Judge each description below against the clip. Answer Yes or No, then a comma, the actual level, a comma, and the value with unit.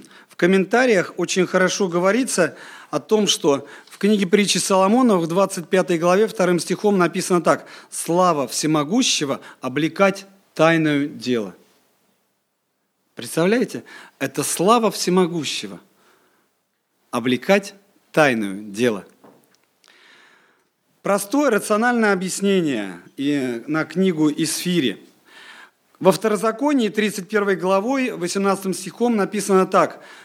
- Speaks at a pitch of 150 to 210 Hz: Yes, medium, 185 Hz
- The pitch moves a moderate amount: Yes, average, 4.1 semitones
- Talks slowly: Yes, slow, 90 wpm